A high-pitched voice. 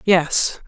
No: medium, 170 Hz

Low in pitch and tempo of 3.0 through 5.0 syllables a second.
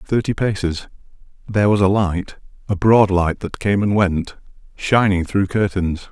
Yes: low, 100 Hz; 4.4 syllables/s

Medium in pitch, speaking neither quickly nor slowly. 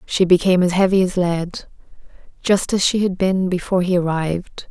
Yes: medium, 180 Hz; average, 165 wpm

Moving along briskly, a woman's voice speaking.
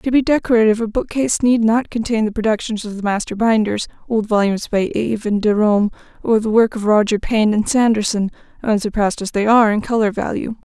No: average, 185 wpm; female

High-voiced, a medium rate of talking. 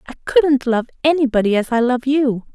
Yes: very high, 260 Hz; average, 190 wpm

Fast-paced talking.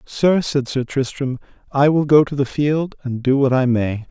Yes: fast, 220 wpm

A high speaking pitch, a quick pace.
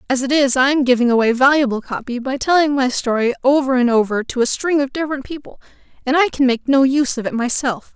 Yes: very high, 265 Hz; fast, 235 wpm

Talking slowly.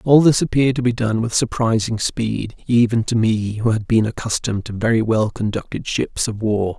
No: fast, 205 wpm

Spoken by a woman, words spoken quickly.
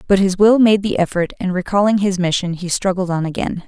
Yes: female; fast, 230 wpm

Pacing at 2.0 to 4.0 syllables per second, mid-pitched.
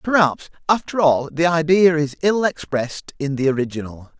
No: 5.1 syllables/s; medium, 155 Hz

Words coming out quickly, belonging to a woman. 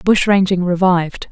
No: slow, 135 wpm; female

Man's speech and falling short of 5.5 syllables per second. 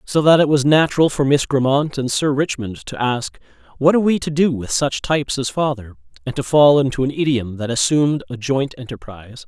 No: male; 5.6 syllables/s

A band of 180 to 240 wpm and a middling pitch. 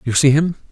No: fast, 250 wpm; medium, 145 Hz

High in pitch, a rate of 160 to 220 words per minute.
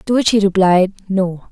Yes: high, 195 Hz; average, 200 wpm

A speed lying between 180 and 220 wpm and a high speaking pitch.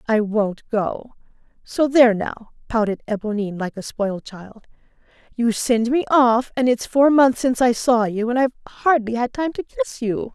Yes: average, 185 wpm; high, 235 Hz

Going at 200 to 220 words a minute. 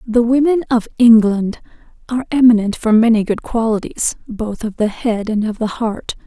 No: average, 170 wpm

